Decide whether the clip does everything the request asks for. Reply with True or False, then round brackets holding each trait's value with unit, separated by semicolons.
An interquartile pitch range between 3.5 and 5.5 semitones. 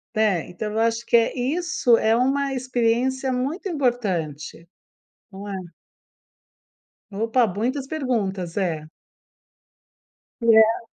True (4.3 semitones)